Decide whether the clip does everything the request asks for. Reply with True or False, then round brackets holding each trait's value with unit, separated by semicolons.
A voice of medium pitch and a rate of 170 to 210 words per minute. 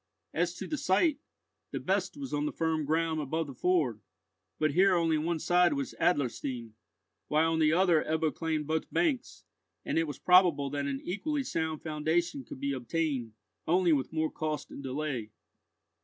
True (160 Hz; 175 wpm)